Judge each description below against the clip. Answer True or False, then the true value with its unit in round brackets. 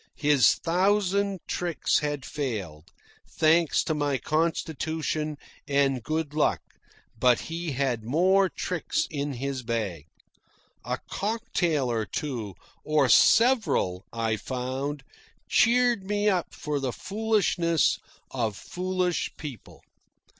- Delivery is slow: True (110 wpm)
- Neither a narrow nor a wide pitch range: False (5.8 semitones)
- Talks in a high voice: False (150 Hz)